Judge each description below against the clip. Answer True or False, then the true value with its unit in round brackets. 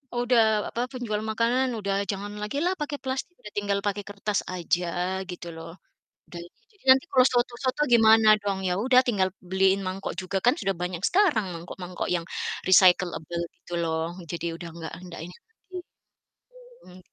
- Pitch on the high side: True (205 Hz)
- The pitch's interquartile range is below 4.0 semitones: False (5.4 semitones)